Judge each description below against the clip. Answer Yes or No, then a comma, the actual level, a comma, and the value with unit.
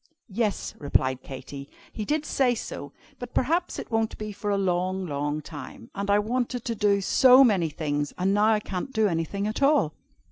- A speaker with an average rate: Yes, average, 190 wpm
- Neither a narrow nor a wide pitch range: No, wide, 6.1 semitones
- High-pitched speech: Yes, high, 200 Hz